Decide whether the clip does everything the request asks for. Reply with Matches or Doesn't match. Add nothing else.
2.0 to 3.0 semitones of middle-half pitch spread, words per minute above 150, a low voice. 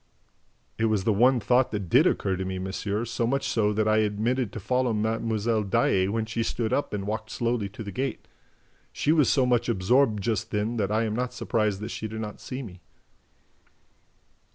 Matches